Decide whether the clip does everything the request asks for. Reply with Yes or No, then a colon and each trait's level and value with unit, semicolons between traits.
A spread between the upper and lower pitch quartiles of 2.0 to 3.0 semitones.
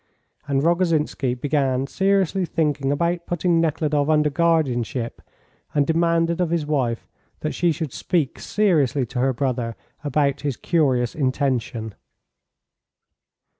No: average, 4.1 semitones